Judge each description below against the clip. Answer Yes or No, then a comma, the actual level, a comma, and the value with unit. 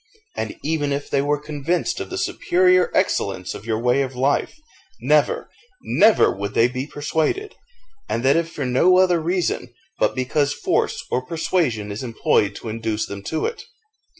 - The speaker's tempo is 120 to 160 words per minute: No, average, 170 wpm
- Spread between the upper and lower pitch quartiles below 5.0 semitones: No, wide, 5.6 semitones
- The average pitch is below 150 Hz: Yes, medium, 140 Hz